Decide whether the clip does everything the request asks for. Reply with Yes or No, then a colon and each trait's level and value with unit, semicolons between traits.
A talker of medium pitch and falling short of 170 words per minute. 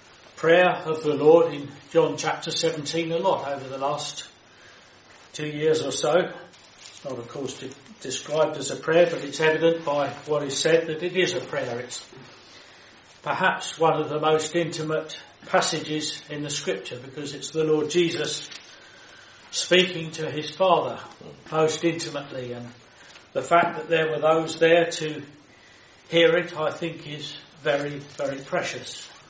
Yes: medium, 155 Hz; average, 160 wpm